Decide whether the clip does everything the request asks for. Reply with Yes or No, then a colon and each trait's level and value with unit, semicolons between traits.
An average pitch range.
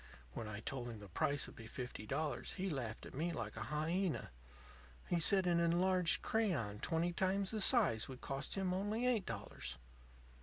No: wide, 7.6 semitones